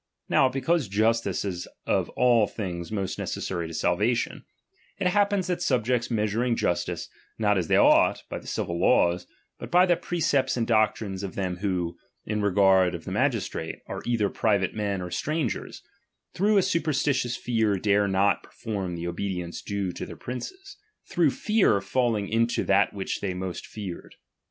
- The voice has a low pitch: Yes, low, 105 Hz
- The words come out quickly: No, average, 170 wpm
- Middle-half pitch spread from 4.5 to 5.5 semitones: Yes, average, 4.9 semitones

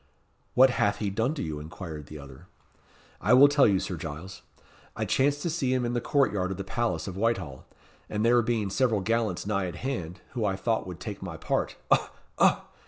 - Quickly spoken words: Yes, fast, 215 wpm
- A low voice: Yes, low, 105 Hz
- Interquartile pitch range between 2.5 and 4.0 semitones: No, average, 5.1 semitones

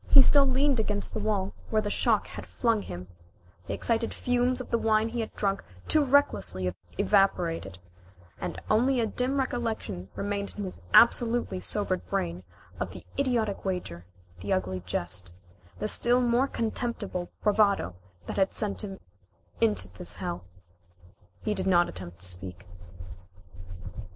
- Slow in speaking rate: No, average, 150 wpm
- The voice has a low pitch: No, high, 205 Hz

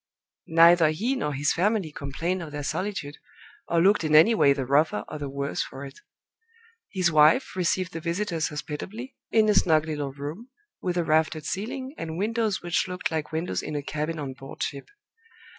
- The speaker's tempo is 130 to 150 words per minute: No, average, 185 wpm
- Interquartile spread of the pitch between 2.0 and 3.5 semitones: No, average, 4.0 semitones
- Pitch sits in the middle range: Yes, medium, 160 Hz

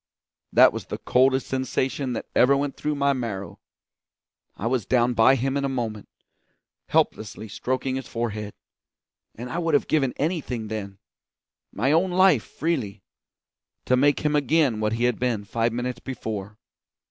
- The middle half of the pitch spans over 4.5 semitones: No, average, 3.8 semitones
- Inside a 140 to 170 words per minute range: Yes, average, 160 wpm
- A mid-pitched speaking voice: No, low, 125 Hz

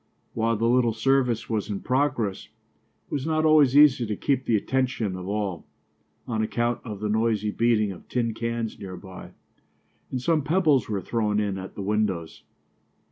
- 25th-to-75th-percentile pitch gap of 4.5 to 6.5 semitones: No, average, 3.5 semitones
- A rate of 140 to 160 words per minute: No, average, 175 wpm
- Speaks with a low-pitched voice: Yes, low, 115 Hz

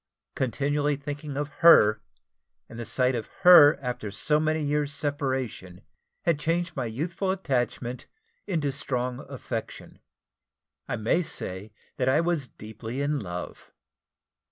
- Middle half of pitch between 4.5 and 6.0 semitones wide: No, average, 3.8 semitones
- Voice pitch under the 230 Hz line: Yes, medium, 140 Hz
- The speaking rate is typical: No, slow, 130 wpm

